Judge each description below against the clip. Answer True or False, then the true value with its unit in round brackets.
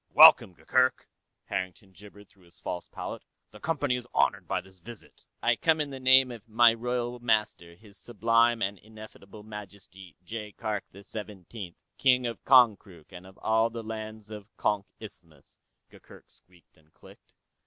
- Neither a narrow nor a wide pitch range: True (3.4 semitones)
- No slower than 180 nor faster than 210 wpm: False (165 wpm)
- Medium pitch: False (110 Hz)